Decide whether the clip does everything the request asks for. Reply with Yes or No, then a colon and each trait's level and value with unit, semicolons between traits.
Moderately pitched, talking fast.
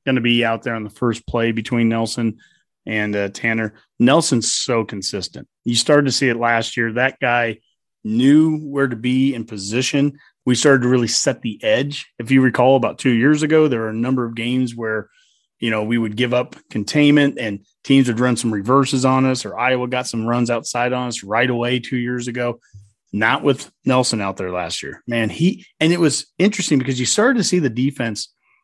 No: low, 125 Hz; fast, 210 wpm